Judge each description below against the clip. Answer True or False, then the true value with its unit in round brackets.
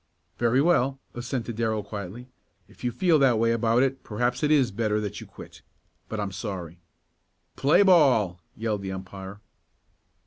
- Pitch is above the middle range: False (115 Hz)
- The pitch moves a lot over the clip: False (4.3 semitones)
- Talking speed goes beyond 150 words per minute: True (160 wpm)